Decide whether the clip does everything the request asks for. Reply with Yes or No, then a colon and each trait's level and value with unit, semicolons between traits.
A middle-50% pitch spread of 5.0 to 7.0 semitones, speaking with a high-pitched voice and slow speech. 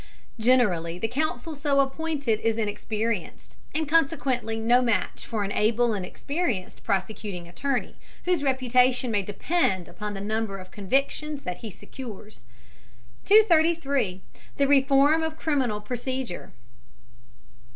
Yes: average, 5.3 semitones; high, 245 Hz; slow, 120 wpm